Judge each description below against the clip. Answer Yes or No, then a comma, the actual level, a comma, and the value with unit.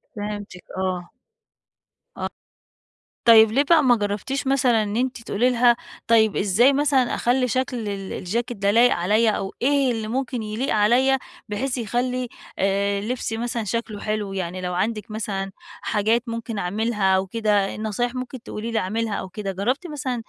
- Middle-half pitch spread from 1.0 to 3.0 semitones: No, average, 3.4 semitones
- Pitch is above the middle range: Yes, high, 225 Hz